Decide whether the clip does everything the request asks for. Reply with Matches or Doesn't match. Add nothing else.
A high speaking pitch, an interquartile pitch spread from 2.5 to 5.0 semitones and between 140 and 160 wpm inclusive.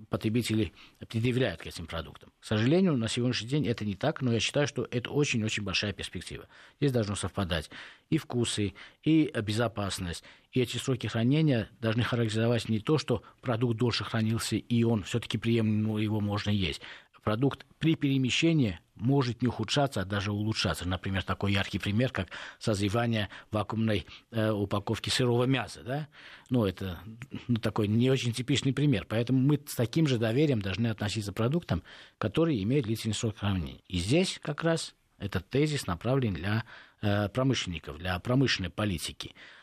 Doesn't match